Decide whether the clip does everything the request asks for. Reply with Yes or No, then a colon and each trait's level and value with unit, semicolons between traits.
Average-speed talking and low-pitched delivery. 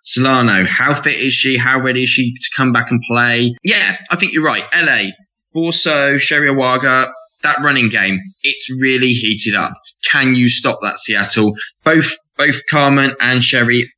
Yes: average, 170 wpm; low, 130 Hz